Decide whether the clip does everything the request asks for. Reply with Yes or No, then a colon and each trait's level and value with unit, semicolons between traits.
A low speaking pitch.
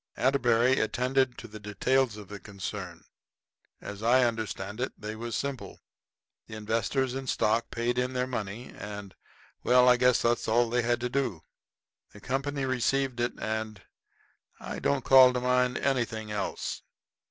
Yes: low, 120 Hz